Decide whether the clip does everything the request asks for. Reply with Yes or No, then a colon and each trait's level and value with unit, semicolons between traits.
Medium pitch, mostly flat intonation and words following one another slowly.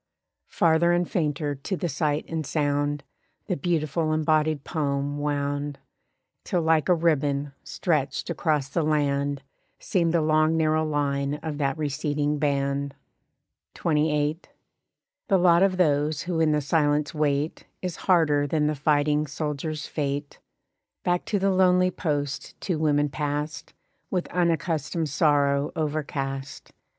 Yes: medium, 150 Hz; narrow, 2.1 semitones; slow, 130 wpm